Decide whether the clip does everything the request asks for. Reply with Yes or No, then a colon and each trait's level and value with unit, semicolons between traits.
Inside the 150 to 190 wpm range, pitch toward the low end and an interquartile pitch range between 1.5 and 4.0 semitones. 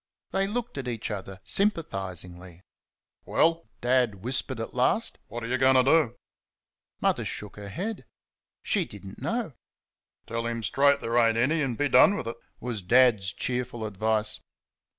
No: average, 160 wpm; low, 120 Hz; average, 4.7 semitones